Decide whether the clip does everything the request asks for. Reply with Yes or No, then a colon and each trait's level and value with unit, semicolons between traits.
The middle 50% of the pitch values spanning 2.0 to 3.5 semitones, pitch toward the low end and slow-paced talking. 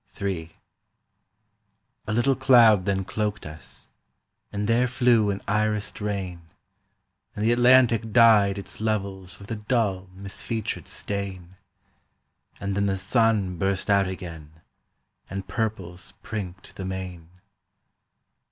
Yes: average, 2.8 semitones; low, 100 Hz; slow, 115 wpm